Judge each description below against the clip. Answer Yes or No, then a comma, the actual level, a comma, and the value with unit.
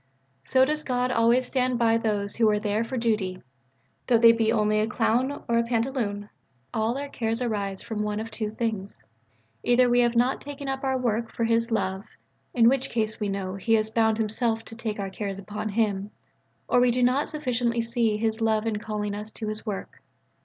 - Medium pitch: No, high, 225 Hz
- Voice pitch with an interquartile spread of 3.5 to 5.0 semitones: No, narrow, 2.4 semitones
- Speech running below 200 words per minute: No, fast, 205 wpm